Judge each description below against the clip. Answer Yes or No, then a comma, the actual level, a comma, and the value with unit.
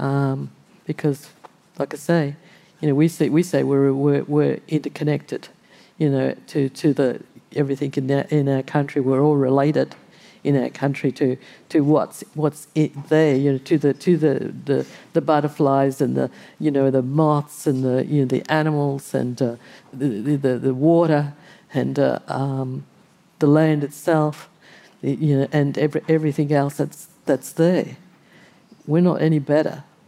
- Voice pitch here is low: No, medium, 145 Hz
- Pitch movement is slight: Yes, narrow, 2.0 semitones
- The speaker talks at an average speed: Yes, average, 150 wpm